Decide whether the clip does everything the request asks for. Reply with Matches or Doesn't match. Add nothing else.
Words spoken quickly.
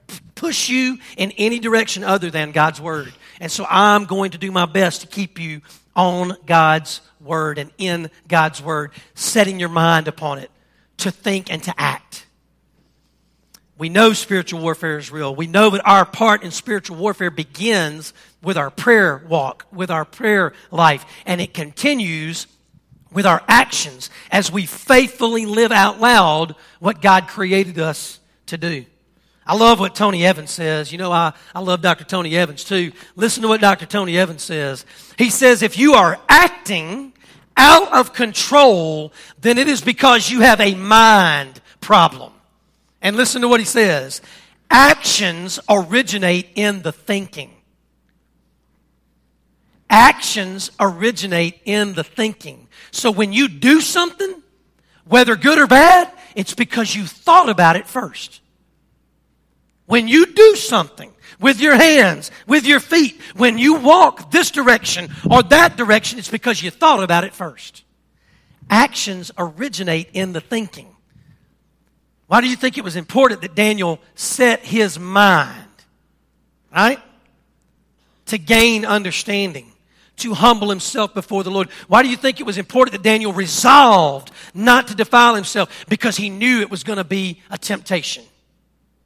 Doesn't match